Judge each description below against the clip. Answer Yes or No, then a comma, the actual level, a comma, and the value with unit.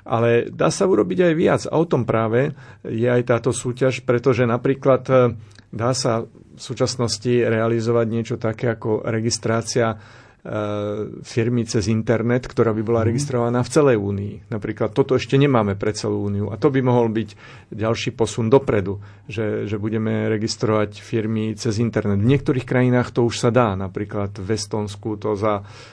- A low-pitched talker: Yes, low, 115 Hz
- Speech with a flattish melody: Yes, narrow, 2.3 semitones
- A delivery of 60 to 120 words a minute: No, average, 160 wpm